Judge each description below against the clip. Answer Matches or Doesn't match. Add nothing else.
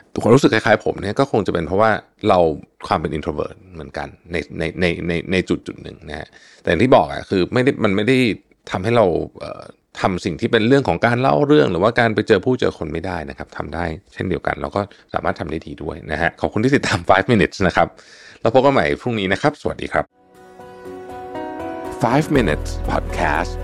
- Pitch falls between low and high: Doesn't match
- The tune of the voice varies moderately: Doesn't match